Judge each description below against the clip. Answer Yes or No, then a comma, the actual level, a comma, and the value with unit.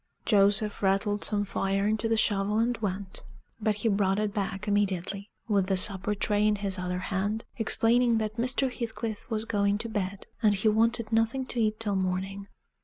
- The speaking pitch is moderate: No, high, 210 Hz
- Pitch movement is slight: Yes, narrow, 2.1 semitones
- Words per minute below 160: No, average, 180 wpm